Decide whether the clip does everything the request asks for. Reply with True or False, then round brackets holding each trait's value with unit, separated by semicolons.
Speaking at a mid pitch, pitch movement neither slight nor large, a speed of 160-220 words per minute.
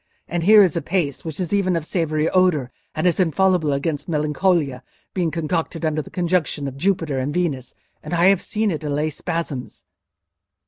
True (165 Hz; 3.4 semitones; 180 wpm)